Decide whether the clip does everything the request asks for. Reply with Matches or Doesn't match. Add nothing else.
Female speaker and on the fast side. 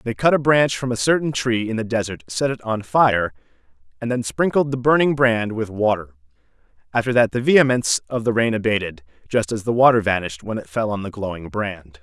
Doesn't match